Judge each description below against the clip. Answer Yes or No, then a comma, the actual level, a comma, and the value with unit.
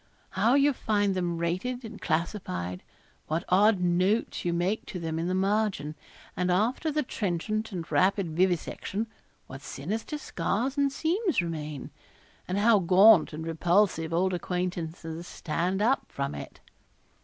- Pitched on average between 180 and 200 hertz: Yes, medium, 185 Hz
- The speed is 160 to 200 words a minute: No, average, 145 wpm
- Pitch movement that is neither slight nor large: Yes, average, 4.4 semitones